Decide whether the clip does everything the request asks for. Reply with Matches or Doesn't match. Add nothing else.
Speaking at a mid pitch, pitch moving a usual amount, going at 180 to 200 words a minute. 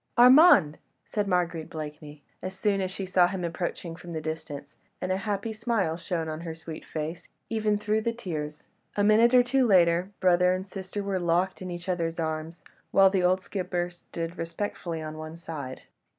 Matches